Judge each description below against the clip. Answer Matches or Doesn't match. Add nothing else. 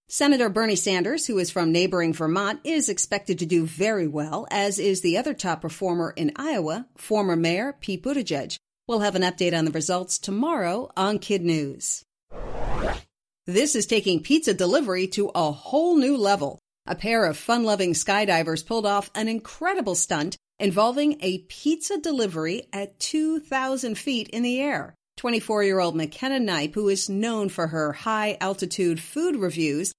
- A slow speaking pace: Doesn't match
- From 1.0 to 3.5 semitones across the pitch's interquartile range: Doesn't match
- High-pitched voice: Matches